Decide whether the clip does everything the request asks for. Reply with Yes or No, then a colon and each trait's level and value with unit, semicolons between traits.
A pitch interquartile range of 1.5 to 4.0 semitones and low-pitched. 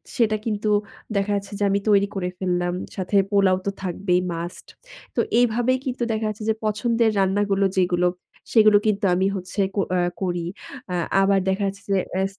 No: narrow, 2.5 semitones; high, 200 Hz